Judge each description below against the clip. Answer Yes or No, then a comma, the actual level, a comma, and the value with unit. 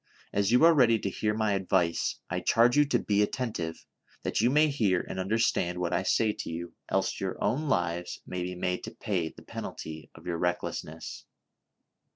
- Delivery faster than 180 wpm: Yes, average, 190 wpm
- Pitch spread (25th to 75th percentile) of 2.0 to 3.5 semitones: No, average, 4.5 semitones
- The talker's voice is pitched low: Yes, very low, 95 Hz